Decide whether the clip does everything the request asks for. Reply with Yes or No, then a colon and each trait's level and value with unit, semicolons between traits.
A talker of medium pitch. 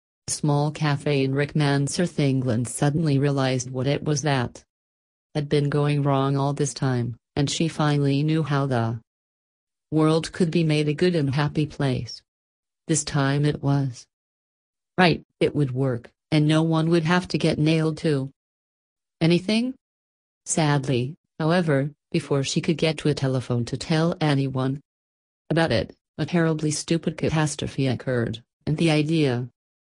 Yes: medium, 145 Hz